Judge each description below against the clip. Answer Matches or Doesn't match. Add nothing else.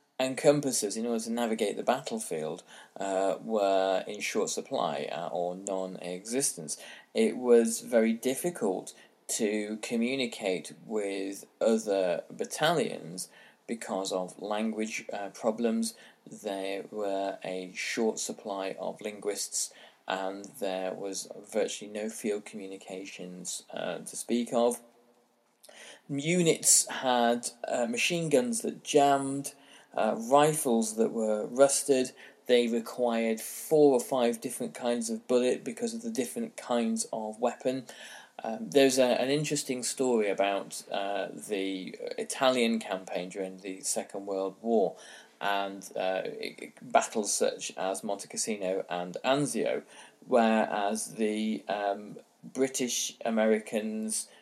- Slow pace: Matches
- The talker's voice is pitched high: Doesn't match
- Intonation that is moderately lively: Matches